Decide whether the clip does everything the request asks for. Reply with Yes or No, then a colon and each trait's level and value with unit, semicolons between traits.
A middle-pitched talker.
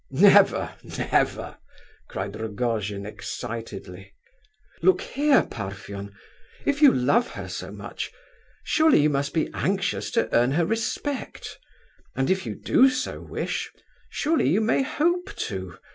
Yes: medium, 155 Hz